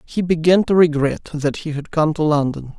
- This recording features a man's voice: Yes, male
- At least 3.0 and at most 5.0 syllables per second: Yes, 4.9 syllables/s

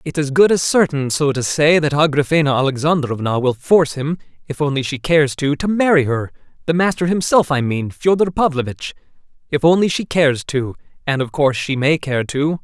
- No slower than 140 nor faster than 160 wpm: No, average, 185 wpm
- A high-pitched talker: No, medium, 145 Hz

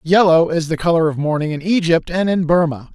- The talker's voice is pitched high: No, medium, 165 Hz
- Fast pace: Yes, fast, 225 wpm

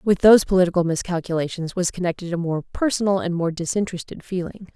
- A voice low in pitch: No, medium, 180 Hz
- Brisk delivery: No, average, 165 wpm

